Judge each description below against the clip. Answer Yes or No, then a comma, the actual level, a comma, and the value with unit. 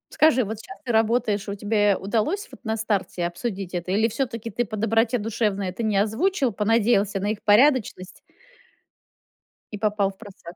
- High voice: Yes, high, 215 Hz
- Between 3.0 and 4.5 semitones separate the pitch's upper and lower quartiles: No, narrow, 2.6 semitones